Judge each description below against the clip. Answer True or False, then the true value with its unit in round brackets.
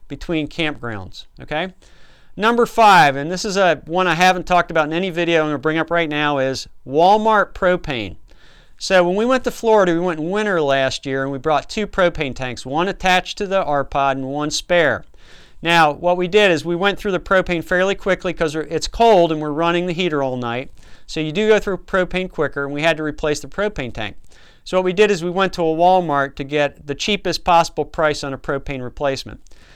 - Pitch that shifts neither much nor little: True (4.6 semitones)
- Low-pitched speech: False (165 Hz)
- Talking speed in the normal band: False (220 wpm)